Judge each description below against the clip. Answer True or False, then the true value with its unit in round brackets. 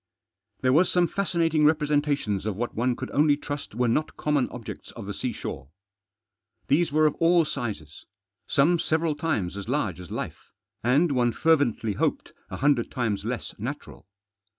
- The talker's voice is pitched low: False (145 Hz)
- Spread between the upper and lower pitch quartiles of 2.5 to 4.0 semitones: False (4.9 semitones)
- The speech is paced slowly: False (160 wpm)